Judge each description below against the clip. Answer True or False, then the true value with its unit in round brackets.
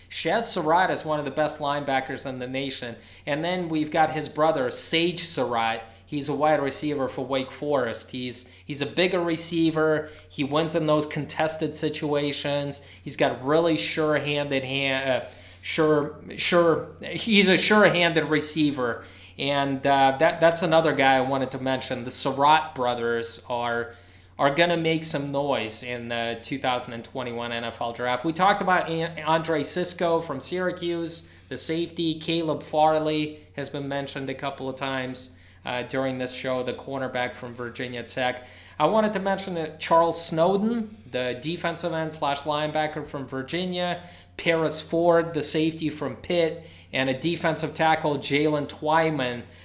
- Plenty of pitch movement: False (4.0 semitones)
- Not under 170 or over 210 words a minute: False (155 wpm)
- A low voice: False (145 Hz)